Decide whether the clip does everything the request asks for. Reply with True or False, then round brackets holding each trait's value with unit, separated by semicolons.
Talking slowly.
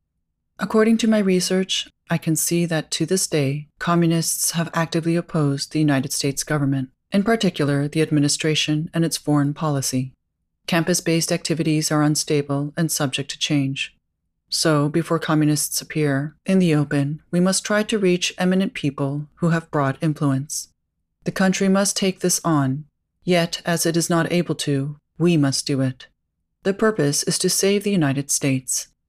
False (165 wpm)